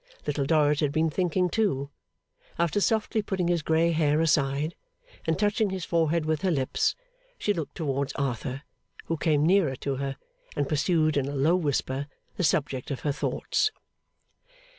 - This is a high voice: No, medium, 155 Hz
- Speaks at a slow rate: No, average, 160 wpm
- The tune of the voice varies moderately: Yes, average, 3.5 semitones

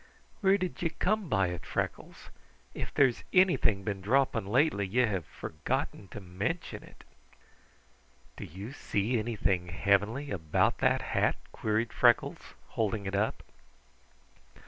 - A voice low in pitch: Yes, low, 110 Hz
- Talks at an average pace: No, slow, 130 wpm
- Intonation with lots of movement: Yes, wide, 5.8 semitones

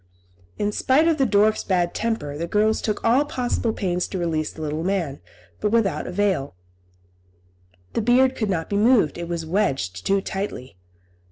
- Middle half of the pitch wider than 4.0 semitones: Yes, average, 5.1 semitones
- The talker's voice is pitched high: Yes, high, 200 Hz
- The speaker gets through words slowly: No, average, 170 wpm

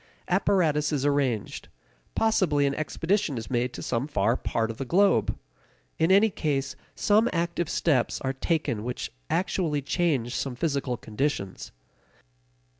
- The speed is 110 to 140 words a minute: Yes, slow, 135 wpm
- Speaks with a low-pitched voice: No, medium, 145 Hz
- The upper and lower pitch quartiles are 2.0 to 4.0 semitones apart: No, wide, 5.5 semitones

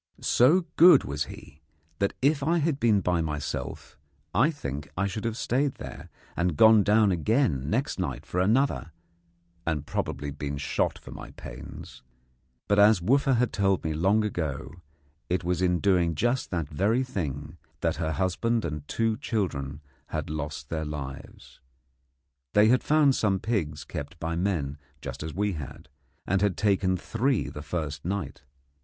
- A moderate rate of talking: Yes, average, 160 wpm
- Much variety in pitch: Yes, wide, 6.7 semitones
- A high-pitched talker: No, very low, 90 Hz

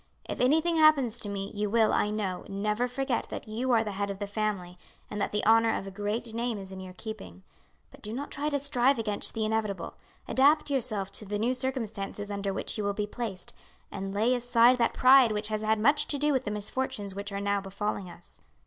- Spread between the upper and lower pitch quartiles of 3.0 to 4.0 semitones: Yes, average, 3.5 semitones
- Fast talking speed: Yes, fast, 230 wpm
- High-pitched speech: Yes, high, 215 Hz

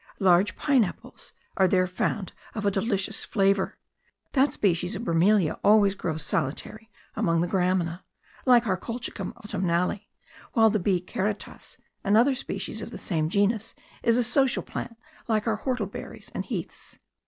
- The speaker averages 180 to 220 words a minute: No, average, 150 wpm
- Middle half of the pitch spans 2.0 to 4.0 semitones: Yes, average, 3.6 semitones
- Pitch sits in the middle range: No, high, 200 Hz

